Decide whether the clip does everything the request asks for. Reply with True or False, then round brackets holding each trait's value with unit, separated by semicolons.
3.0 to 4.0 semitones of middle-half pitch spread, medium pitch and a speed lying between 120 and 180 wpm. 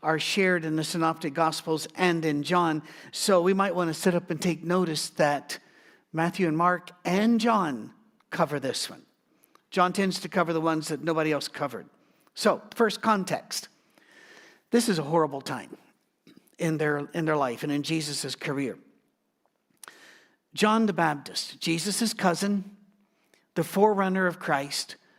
True (3.7 semitones; 170 Hz; 150 wpm)